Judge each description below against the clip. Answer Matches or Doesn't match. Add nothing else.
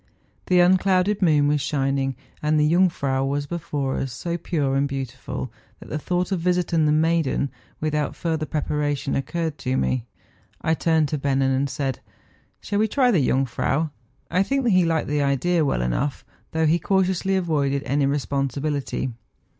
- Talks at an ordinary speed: Matches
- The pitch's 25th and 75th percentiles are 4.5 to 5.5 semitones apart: Doesn't match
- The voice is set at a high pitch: Doesn't match